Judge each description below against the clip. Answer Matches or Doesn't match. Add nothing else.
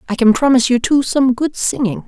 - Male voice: Doesn't match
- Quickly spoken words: Matches